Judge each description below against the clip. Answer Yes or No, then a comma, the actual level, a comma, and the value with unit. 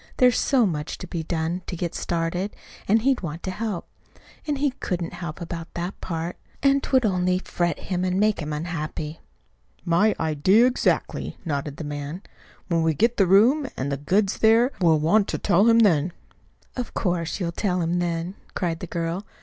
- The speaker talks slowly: No, average, 185 wpm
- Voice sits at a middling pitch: Yes, medium, 175 Hz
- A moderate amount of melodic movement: Yes, average, 4.1 semitones